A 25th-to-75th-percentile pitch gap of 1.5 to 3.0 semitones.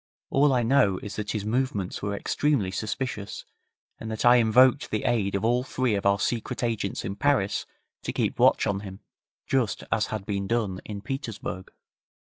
No: average, 3.8 semitones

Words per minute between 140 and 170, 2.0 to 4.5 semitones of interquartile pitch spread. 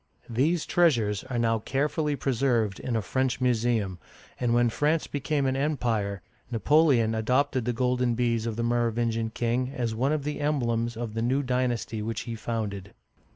Yes: average, 165 wpm; average, 2.8 semitones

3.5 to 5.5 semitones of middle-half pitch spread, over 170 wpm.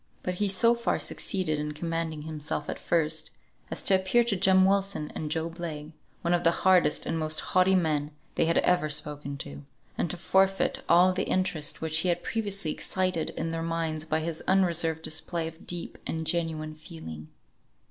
No: average, 3.0 semitones; average, 185 wpm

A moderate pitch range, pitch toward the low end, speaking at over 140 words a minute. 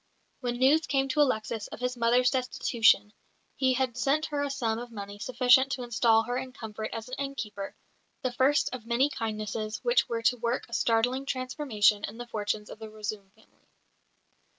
No: average, 3.0 semitones; high, 240 Hz; average, 185 wpm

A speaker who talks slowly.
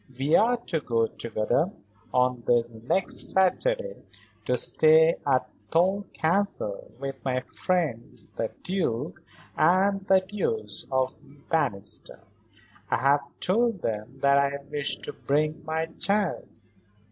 Yes: slow, 120 wpm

